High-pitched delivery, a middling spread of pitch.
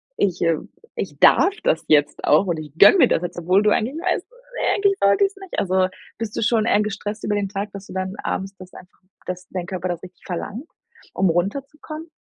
Yes: high, 195 Hz; average, 3.6 semitones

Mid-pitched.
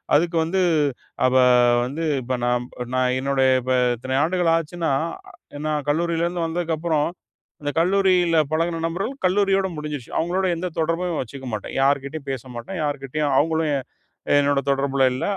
Yes: medium, 155 Hz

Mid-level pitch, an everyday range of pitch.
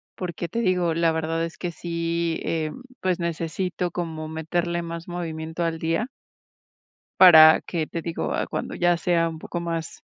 No: medium, 170 Hz; narrow, 1.3 semitones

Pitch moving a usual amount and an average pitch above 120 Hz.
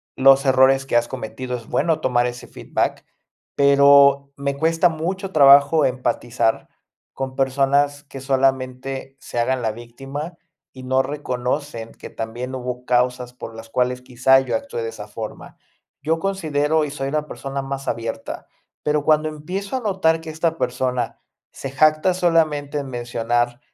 Yes: average, 3.2 semitones; low, 135 Hz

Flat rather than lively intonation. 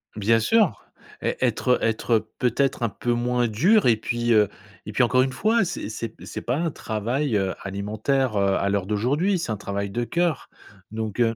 No: average, 4.0 semitones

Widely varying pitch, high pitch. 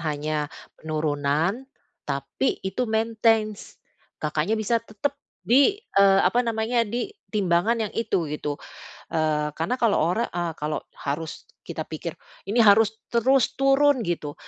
Yes: wide, 6.9 semitones; high, 205 Hz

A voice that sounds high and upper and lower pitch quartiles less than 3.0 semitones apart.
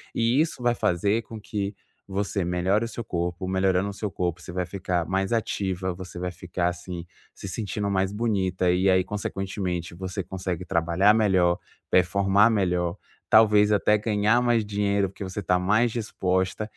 No: very low, 95 Hz; narrow, 2.4 semitones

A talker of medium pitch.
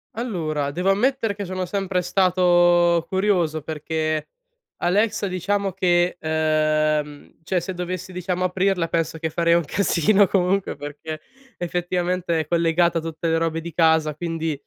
Yes: medium, 175 Hz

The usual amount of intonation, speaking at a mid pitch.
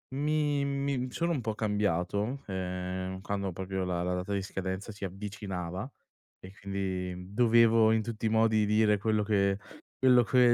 No: average, 3.4 semitones; low, 105 Hz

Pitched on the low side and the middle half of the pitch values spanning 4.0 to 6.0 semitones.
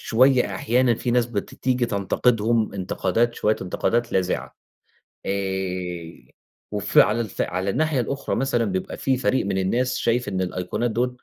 Yes: low, 115 Hz; average, 4.5 semitones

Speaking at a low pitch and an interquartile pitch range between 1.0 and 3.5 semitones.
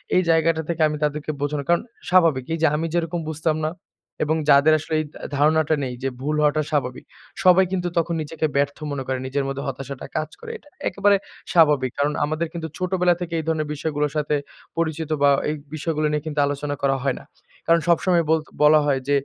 No: medium, 155 Hz; narrow, 2.5 semitones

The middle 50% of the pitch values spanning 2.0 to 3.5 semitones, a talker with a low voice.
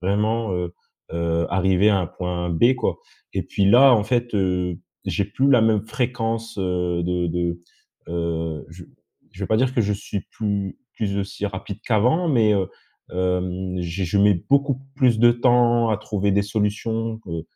No: average, 4.1 semitones; low, 100 Hz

